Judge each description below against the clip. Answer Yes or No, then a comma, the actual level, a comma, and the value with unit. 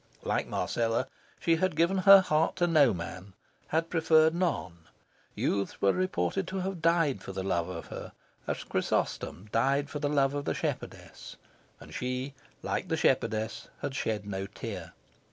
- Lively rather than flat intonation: Yes, wide, 7.8 semitones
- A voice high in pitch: No, medium, 140 Hz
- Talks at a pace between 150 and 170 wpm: Yes, average, 155 wpm